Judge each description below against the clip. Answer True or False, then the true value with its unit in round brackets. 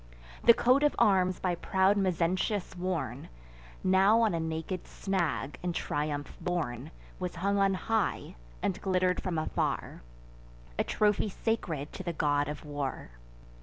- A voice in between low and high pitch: True (180 Hz)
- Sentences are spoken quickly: False (140 wpm)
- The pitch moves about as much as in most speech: True (3.5 semitones)